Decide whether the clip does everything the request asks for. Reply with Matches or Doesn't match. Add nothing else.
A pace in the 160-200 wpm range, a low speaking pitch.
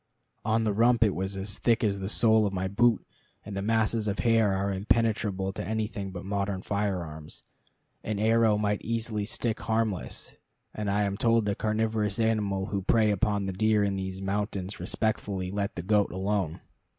Matches